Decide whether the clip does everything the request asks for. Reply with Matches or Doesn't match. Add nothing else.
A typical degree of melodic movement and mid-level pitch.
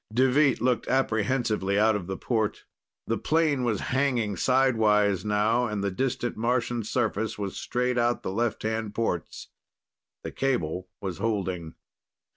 Doesn't match